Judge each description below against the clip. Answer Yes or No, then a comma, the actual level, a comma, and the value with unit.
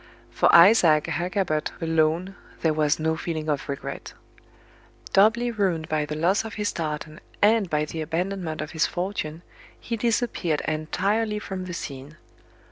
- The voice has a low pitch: No, medium, 165 Hz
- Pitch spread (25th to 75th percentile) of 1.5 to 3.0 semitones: No, average, 4.3 semitones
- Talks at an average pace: Yes, average, 145 wpm